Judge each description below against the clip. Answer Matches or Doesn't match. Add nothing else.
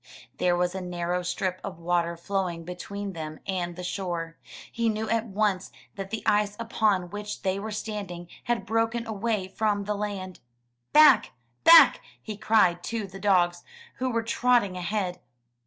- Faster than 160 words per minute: Doesn't match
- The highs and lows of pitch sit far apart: Doesn't match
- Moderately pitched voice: Doesn't match